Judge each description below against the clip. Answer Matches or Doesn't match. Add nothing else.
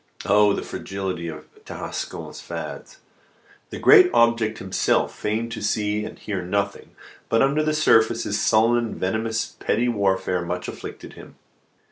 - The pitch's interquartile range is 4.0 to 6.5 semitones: Doesn't match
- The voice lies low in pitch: Matches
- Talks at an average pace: Matches